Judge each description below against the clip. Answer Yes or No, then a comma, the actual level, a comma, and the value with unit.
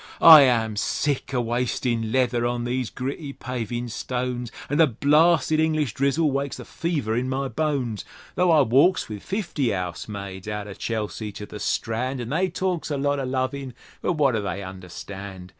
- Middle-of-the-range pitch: No, low, 125 Hz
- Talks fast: No, average, 175 wpm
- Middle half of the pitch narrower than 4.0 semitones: No, average, 4.4 semitones